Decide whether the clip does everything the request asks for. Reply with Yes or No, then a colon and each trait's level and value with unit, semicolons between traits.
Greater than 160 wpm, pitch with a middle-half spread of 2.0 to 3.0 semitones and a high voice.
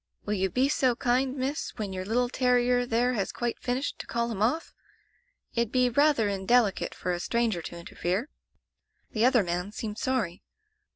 No: average, 175 wpm; average, 3.8 semitones; high, 235 Hz